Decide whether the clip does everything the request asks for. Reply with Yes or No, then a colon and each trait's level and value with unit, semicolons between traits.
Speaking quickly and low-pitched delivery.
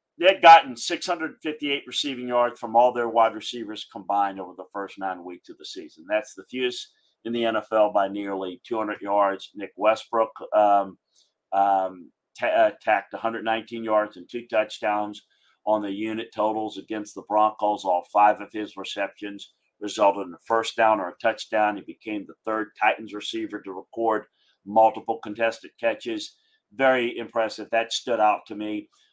No: average, 165 wpm; low, 110 Hz